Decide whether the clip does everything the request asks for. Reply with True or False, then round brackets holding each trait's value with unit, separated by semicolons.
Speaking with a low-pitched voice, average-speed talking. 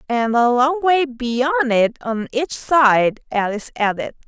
False (255 Hz; 155 wpm)